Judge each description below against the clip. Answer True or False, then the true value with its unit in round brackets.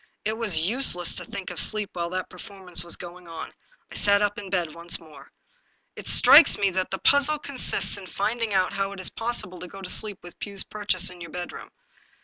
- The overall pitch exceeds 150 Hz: True (190 Hz)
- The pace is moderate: False (220 wpm)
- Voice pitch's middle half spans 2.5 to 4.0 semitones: True (2.8 semitones)